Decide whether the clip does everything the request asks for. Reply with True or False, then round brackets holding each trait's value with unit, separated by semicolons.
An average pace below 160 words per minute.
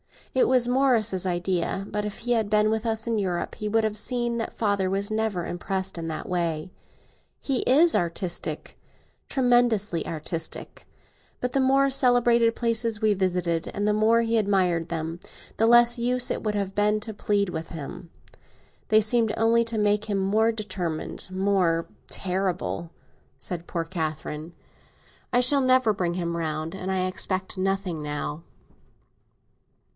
True (150 wpm)